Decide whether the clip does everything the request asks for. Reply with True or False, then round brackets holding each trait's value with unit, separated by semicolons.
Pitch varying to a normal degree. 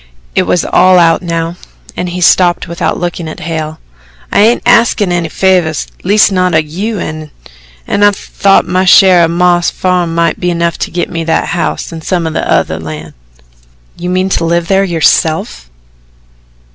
False (2.0 semitones)